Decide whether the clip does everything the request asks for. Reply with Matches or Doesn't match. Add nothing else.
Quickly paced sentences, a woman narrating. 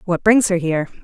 Matches